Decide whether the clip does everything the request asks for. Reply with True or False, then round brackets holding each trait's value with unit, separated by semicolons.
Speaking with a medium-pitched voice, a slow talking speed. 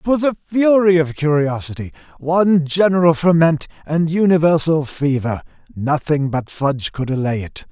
True (160 Hz; 125 wpm)